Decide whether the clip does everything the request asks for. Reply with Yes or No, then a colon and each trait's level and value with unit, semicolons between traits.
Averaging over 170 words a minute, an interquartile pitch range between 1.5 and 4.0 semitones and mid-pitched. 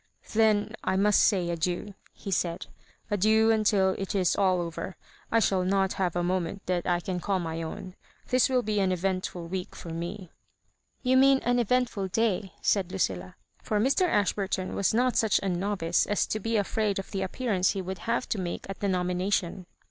No: average, 195 wpm; average, 2.9 semitones; high, 195 Hz